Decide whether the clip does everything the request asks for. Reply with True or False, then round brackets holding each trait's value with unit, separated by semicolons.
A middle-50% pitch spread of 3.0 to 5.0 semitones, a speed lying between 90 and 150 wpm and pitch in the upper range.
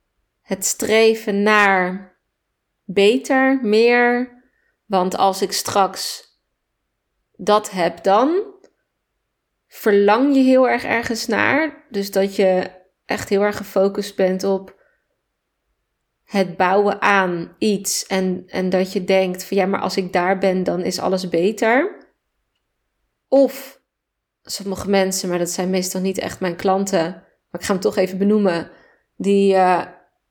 False (2.6 semitones; 135 wpm; 195 Hz)